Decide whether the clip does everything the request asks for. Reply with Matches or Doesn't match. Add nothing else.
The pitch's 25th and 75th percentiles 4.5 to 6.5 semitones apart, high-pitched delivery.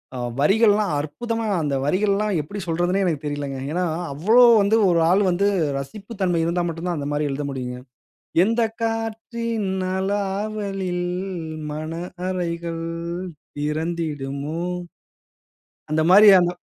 Doesn't match